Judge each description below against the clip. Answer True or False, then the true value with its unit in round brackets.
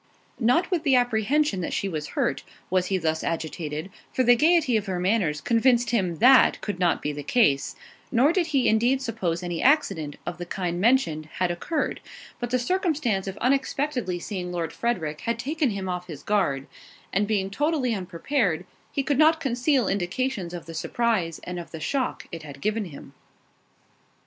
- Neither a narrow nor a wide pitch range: False (6.8 semitones)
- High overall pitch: True (205 Hz)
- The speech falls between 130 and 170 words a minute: False (180 wpm)